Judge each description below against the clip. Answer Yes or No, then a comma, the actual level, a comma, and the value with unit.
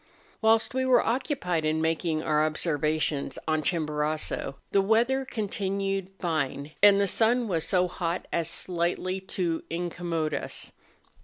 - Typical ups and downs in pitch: Yes, average, 4.2 semitones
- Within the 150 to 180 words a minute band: No, average, 140 wpm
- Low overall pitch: No, medium, 175 Hz